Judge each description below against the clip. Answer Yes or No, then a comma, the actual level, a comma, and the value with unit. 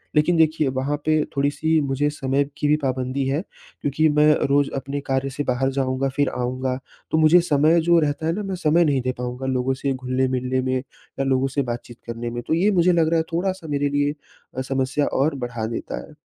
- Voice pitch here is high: No, medium, 140 Hz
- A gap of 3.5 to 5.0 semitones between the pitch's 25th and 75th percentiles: No, average, 3.1 semitones